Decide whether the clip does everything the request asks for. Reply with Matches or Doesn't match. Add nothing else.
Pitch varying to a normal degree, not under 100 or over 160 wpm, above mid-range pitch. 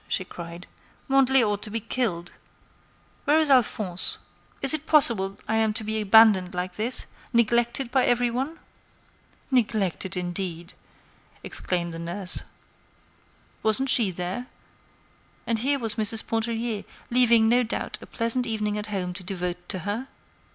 Matches